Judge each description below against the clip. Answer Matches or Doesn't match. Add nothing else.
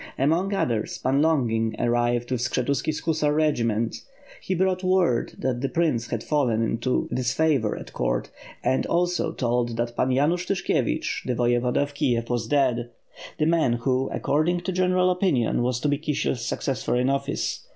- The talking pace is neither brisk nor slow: Matches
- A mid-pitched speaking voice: Doesn't match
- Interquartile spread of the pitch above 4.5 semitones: Matches